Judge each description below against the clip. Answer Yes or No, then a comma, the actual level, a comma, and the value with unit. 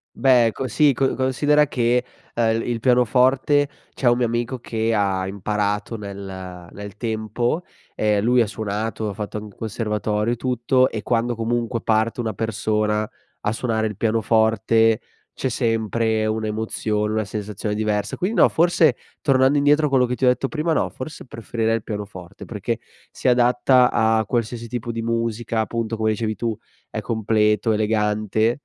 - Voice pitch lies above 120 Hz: No, low, 115 Hz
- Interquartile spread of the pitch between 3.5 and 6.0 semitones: No, narrow, 2.3 semitones